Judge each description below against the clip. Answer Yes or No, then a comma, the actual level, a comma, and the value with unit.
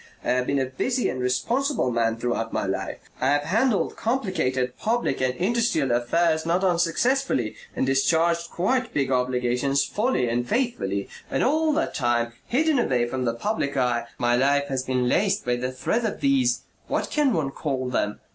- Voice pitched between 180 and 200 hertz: No, medium, 140 Hz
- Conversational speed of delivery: Yes, average, 175 wpm